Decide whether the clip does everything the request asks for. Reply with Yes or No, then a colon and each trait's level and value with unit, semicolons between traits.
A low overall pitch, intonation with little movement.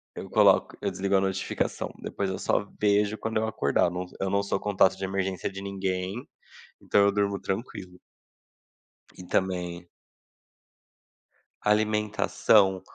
Yes: very low, 95 Hz; narrow, 1.6 semitones